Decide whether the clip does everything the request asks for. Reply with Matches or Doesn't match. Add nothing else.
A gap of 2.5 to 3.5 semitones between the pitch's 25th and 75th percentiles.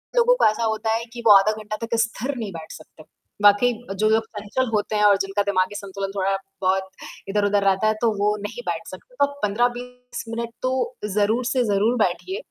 Matches